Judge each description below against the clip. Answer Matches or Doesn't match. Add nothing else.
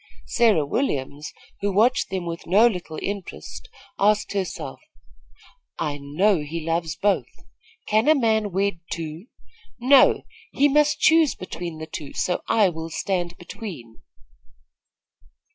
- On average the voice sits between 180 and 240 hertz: Matches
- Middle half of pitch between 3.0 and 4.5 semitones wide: Doesn't match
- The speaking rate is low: Matches